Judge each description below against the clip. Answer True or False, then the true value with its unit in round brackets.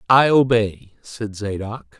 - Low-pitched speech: True (110 Hz)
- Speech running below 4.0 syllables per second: True (3.5 syllables/s)